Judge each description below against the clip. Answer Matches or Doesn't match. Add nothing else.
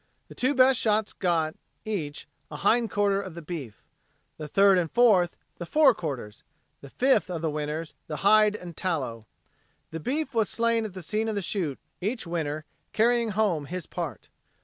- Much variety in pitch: Matches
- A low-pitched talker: Doesn't match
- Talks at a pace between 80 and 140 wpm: Doesn't match